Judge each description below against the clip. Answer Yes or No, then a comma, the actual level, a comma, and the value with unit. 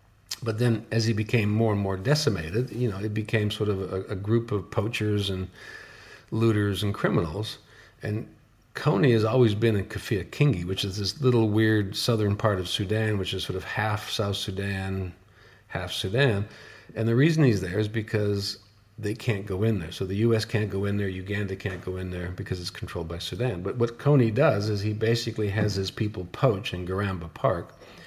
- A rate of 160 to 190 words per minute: No, average, 200 wpm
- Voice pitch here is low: Yes, low, 105 Hz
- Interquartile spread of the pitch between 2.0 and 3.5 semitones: Yes, narrow, 2.5 semitones